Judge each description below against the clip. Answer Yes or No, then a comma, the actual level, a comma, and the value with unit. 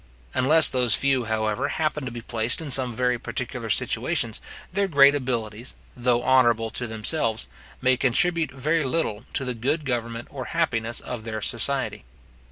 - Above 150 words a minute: Yes, average, 160 wpm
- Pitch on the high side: No, low, 125 Hz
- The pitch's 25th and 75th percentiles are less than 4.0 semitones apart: Yes, average, 3.3 semitones